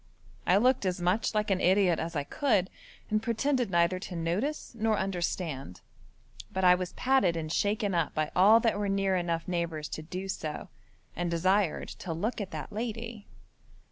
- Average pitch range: Yes, average, 3.9 semitones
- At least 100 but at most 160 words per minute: No, average, 175 wpm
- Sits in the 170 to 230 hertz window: Yes, medium, 185 Hz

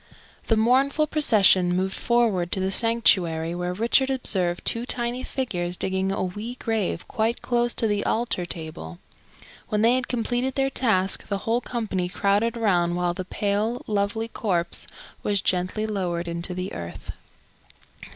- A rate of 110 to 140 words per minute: No, average, 150 wpm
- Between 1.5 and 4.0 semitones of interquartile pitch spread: No, average, 4.7 semitones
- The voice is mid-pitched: No, high, 205 Hz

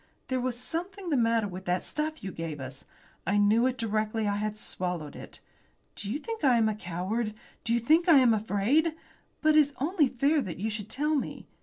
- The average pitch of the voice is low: No, high, 230 Hz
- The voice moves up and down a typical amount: No, wide, 6.2 semitones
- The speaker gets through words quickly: Yes, fast, 215 wpm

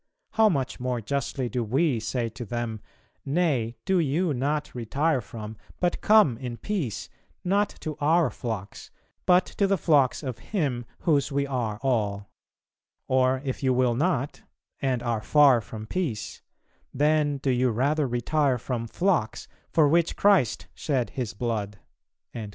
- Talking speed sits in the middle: Yes, average, 150 wpm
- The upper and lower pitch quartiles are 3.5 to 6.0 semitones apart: Yes, average, 4.6 semitones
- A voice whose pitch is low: Yes, low, 130 Hz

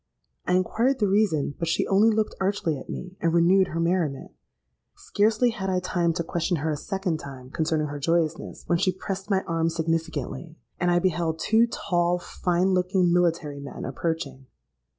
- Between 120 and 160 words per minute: No, average, 175 wpm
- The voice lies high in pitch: No, medium, 175 Hz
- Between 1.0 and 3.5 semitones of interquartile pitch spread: Yes, average, 2.9 semitones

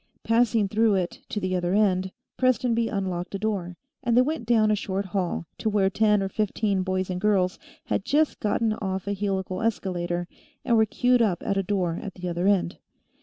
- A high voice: Yes, high, 200 Hz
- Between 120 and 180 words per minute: No, average, 200 wpm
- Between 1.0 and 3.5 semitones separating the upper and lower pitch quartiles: Yes, average, 2.9 semitones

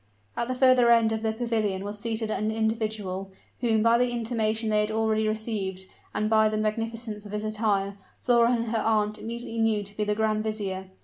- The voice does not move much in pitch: Yes, narrow, 1.4 semitones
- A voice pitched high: Yes, high, 220 Hz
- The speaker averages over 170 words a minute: Yes, average, 200 wpm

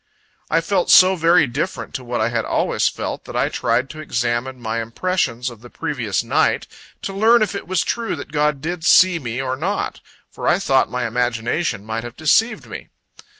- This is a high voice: No, low, 135 Hz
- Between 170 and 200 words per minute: Yes, average, 195 wpm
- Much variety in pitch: Yes, wide, 7.0 semitones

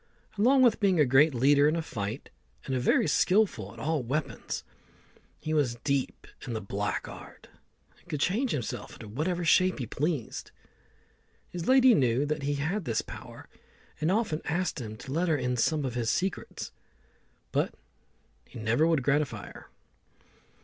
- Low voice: No, medium, 150 Hz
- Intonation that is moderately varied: No, wide, 5.7 semitones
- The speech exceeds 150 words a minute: Yes, average, 165 wpm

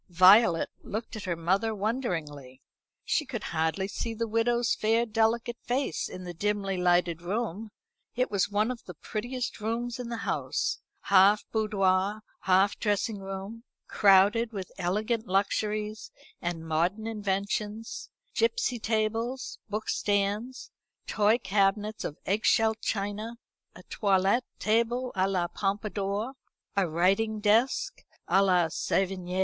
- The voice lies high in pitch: Yes, high, 210 Hz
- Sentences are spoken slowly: Yes, slow, 130 wpm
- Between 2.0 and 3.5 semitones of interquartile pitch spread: Yes, average, 2.9 semitones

